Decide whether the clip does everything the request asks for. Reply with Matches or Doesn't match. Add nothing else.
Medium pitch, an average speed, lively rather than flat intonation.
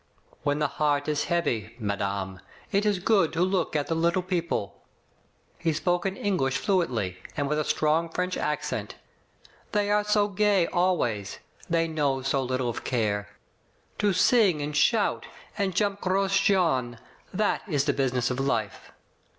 Matches